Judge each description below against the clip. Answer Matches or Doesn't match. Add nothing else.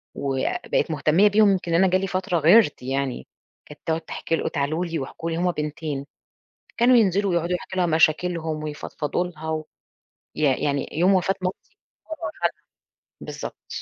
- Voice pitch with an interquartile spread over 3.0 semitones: Matches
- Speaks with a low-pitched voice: Doesn't match